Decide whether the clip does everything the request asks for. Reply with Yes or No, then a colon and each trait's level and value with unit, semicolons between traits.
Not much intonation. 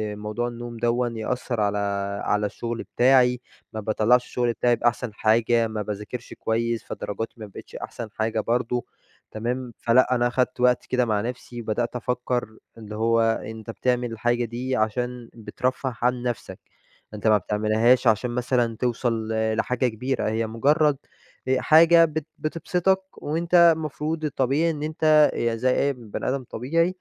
Yes: narrow, 2.3 semitones